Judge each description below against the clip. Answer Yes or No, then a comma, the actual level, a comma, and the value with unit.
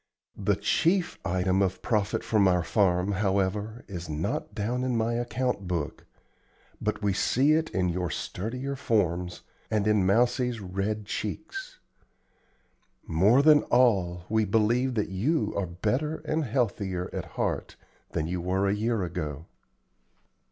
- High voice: No, low, 105 Hz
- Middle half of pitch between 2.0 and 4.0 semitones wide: No, average, 4.9 semitones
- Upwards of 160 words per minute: No, average, 140 wpm